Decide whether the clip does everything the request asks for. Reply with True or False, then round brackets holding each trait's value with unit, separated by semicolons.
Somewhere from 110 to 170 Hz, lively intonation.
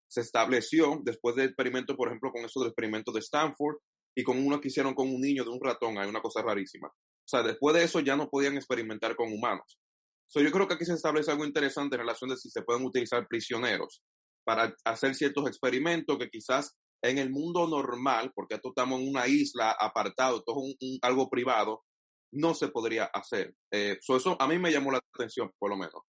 False (135 Hz; 3.3 semitones)